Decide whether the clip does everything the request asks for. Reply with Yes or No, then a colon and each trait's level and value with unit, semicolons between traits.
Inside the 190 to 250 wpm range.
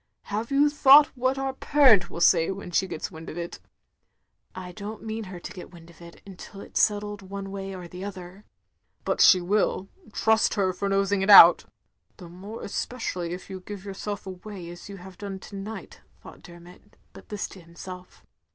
Yes: fast, 205 wpm